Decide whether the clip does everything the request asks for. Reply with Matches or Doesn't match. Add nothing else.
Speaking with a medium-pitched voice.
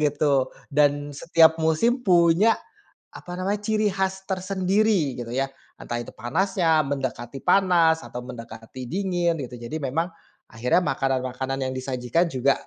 Matches